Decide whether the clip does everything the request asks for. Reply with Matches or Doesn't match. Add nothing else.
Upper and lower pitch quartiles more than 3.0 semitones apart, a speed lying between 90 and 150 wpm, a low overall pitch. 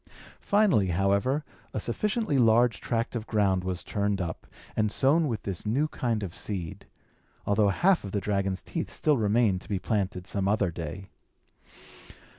Doesn't match